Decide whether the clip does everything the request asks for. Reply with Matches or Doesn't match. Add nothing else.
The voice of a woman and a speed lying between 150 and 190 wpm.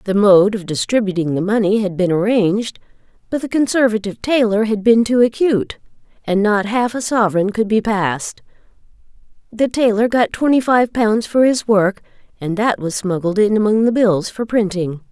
Matches